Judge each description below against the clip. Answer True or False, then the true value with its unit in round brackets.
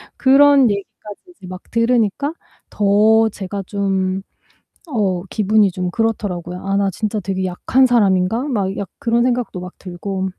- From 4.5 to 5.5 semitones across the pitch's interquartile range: False (3.3 semitones)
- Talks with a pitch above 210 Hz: False (200 Hz)